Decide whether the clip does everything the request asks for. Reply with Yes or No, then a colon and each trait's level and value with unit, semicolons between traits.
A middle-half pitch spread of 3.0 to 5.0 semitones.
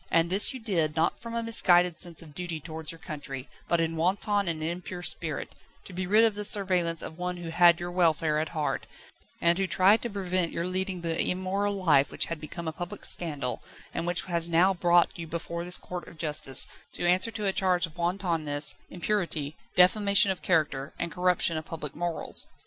No: narrow, 2.4 semitones